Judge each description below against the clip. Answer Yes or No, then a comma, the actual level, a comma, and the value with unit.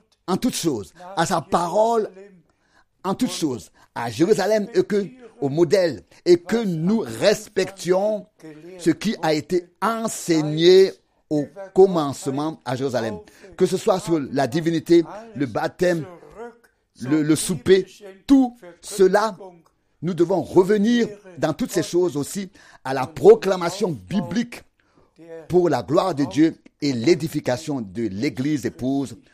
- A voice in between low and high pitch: Yes, medium, 180 Hz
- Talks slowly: Yes, slow, 130 wpm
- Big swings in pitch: No, average, 4.4 semitones